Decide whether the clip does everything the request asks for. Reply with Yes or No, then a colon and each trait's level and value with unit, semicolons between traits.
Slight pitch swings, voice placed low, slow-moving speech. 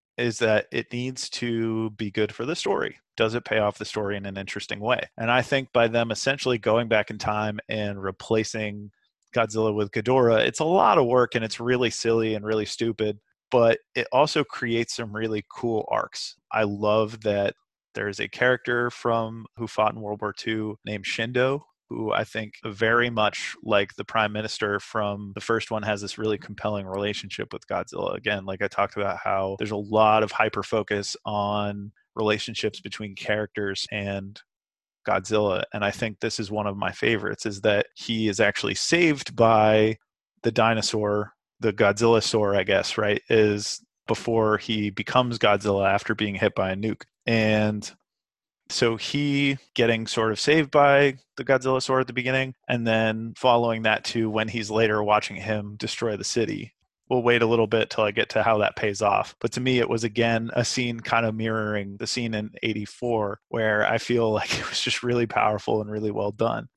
No: narrow, 1.9 semitones; low, 110 Hz; average, 190 wpm